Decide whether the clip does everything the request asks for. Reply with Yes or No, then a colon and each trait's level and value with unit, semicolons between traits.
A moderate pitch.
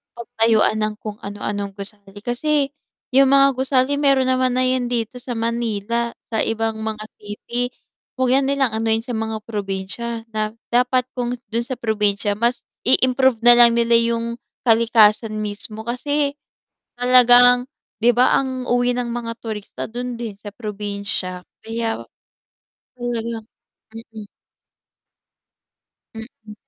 No: high, 235 Hz